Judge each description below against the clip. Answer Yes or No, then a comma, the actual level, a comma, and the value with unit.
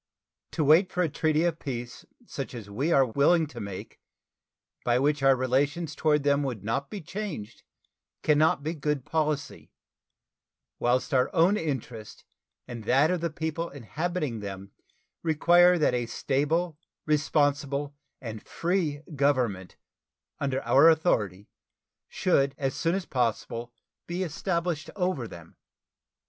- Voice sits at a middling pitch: Yes, medium, 145 Hz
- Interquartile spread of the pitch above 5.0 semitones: No, average, 4.6 semitones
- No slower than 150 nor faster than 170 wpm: No, slow, 135 wpm